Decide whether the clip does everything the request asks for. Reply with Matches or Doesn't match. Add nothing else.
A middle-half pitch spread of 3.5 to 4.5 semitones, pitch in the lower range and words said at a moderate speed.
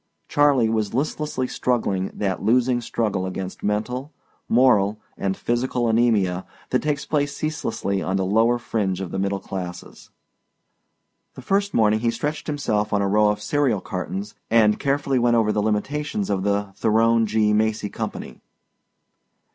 Matches